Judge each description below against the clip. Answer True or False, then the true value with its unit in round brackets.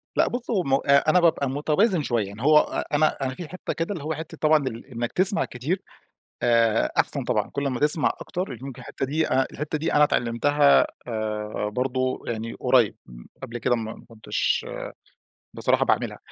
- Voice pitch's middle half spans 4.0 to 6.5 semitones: True (4.7 semitones)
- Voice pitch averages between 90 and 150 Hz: True (135 Hz)